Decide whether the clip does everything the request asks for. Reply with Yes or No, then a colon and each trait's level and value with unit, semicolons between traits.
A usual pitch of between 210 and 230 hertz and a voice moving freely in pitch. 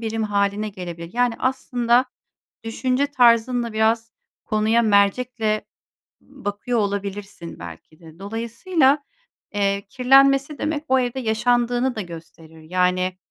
No: high, 225 Hz; average, 3.8 semitones